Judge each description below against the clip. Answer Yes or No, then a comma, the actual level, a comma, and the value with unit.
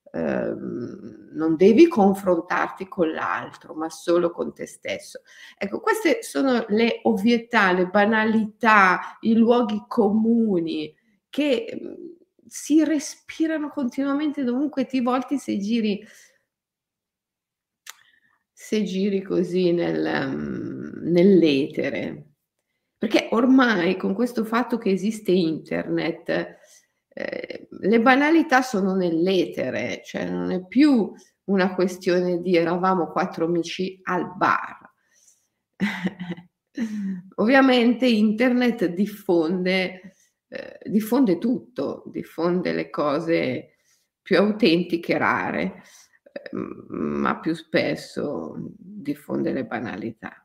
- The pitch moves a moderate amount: No, wide, 5.7 semitones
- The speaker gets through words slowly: Yes, slow, 100 wpm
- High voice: Yes, high, 205 Hz